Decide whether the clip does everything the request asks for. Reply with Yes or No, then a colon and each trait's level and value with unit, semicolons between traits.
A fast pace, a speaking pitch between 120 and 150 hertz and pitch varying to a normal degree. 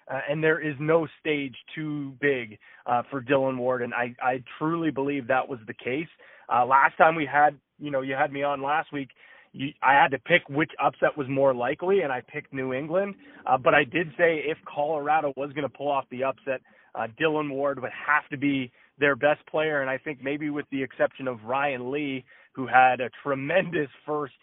No: fast, 215 wpm; medium, 140 Hz; narrow, 2.3 semitones